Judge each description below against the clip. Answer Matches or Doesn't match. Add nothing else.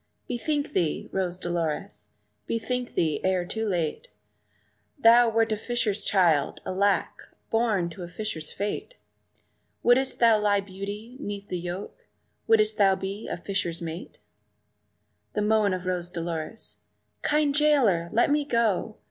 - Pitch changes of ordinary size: Matches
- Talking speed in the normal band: Doesn't match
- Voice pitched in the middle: Doesn't match